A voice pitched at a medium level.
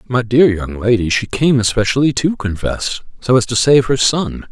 No: low, 120 Hz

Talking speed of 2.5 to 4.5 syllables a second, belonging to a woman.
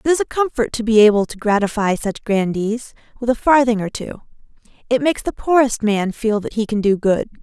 No: 5.7 syllables/s; female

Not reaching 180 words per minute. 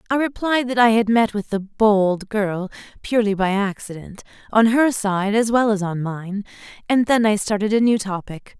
No: average, 195 wpm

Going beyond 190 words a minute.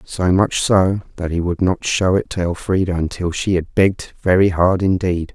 Yes: average, 200 wpm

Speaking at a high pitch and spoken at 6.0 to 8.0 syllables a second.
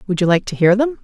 Yes: high, 205 Hz; 7.0 syllables/s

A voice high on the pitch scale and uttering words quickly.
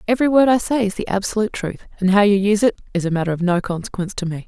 Yes: high, 200 Hz; fast, 280 wpm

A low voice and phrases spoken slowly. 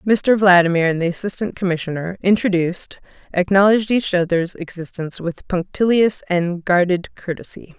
No: medium, 185 Hz; slow, 125 wpm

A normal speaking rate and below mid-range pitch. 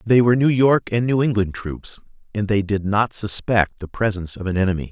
No: fast, 220 wpm; low, 105 Hz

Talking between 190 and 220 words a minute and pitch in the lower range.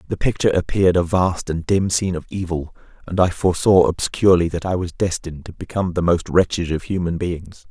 Yes: average, 200 wpm; very low, 90 Hz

